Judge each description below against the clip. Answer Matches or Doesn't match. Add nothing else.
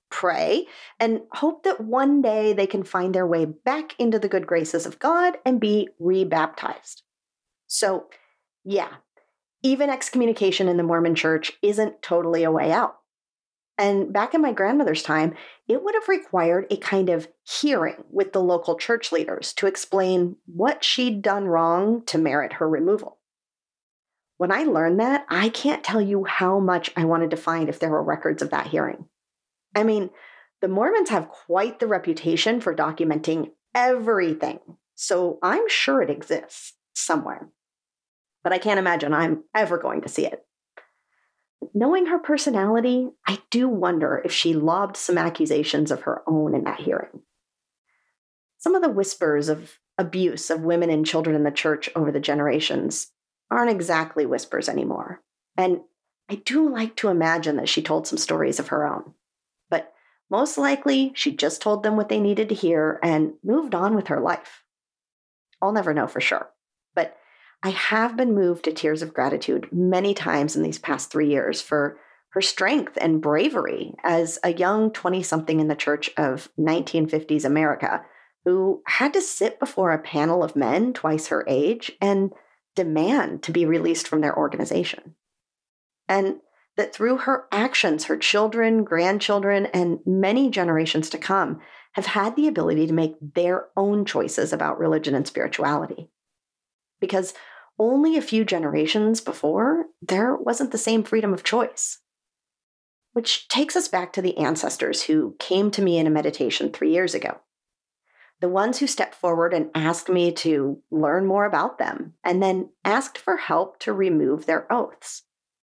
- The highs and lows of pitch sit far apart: Matches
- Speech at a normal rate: Matches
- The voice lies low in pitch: Doesn't match